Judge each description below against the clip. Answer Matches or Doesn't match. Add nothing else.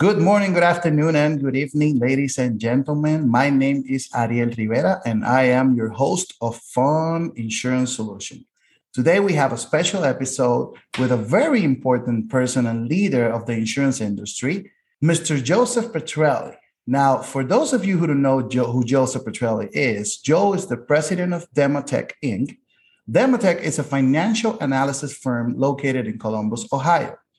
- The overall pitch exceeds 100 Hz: Matches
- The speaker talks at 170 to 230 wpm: Doesn't match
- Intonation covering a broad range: Doesn't match